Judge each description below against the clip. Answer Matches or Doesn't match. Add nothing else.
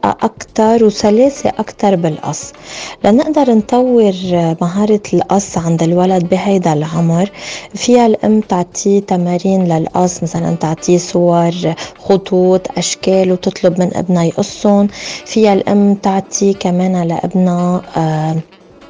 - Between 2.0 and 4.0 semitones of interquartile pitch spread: Matches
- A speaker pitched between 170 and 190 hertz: Matches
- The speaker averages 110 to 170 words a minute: Doesn't match